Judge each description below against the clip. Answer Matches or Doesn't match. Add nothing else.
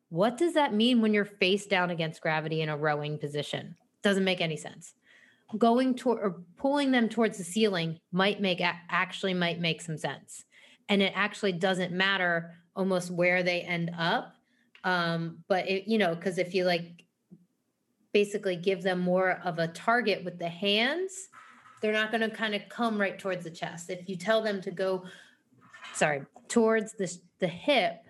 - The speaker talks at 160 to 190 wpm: Matches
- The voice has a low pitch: Doesn't match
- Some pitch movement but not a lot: Matches